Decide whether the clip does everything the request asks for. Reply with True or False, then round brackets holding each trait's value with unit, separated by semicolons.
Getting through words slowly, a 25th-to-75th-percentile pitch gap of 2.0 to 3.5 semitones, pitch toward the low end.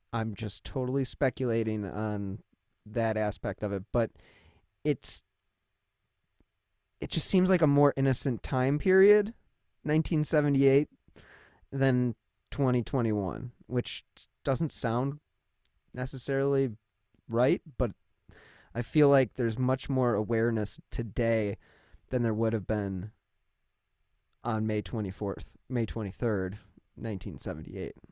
False (100 wpm; 4.5 semitones; 115 Hz)